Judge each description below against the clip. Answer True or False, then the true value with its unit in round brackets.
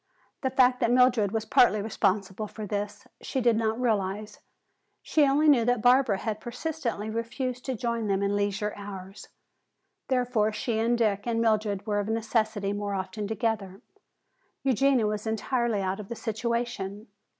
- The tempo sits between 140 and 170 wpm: True (160 wpm)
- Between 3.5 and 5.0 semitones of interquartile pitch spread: False (2.9 semitones)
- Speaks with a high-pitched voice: True (220 Hz)